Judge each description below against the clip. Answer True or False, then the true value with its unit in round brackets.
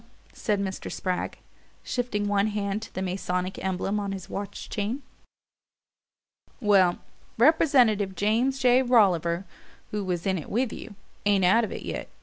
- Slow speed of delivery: False (145 wpm)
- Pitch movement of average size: True (3.2 semitones)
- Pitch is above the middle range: True (205 Hz)